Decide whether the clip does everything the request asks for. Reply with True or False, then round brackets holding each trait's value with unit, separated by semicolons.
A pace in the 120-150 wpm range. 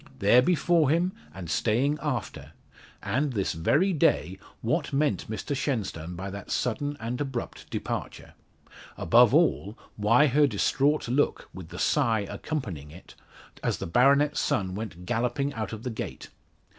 True (145 wpm)